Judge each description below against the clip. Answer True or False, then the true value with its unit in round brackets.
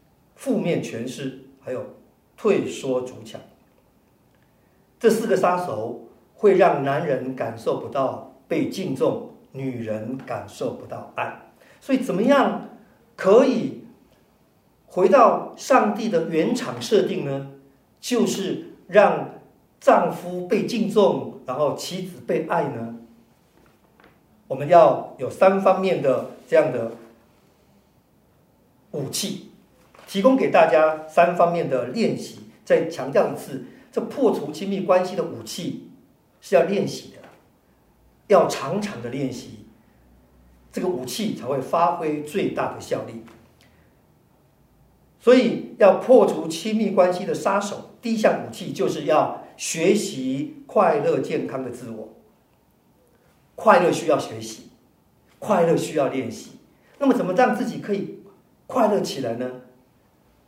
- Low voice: False (175 Hz)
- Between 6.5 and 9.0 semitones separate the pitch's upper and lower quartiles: True (8.5 semitones)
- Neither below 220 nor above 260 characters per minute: False (180 characters per minute)